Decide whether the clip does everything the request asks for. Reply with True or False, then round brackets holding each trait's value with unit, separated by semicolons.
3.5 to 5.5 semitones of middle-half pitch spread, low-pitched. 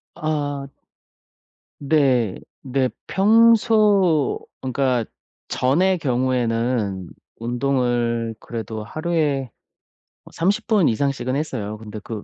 True (5.1 semitones; 130 Hz)